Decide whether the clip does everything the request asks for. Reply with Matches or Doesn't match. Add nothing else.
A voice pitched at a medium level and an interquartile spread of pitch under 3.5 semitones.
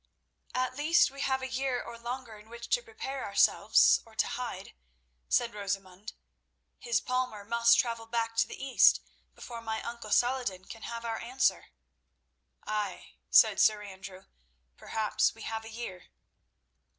Doesn't match